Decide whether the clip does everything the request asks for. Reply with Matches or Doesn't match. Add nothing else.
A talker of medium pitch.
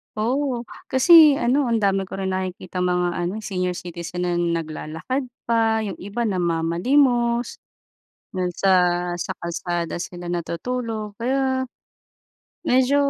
Doesn't match